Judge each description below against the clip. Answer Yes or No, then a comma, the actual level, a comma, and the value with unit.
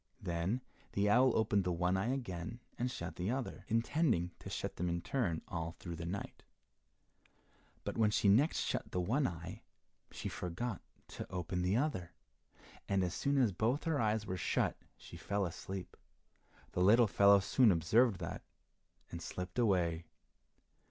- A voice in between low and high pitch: No, low, 100 Hz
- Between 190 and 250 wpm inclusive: No, average, 165 wpm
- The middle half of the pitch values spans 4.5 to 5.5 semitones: Yes, average, 5.1 semitones